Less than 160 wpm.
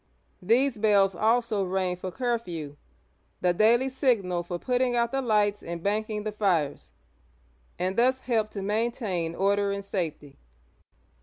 Yes: average, 150 wpm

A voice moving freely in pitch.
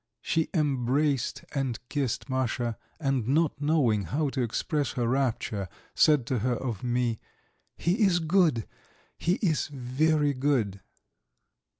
No: average, 4.0 semitones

